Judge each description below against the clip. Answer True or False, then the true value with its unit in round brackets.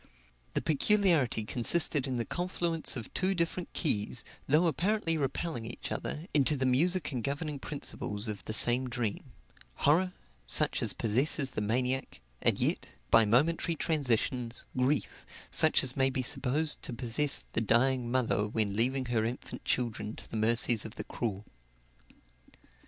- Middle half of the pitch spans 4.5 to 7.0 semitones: True (4.9 semitones)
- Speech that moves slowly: False (150 wpm)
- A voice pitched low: True (130 Hz)